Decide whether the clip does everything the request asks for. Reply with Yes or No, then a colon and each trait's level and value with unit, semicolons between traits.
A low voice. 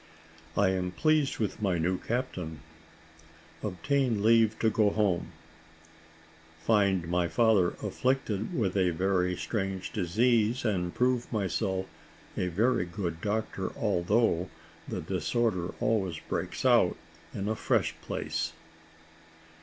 Yes: low, 100 Hz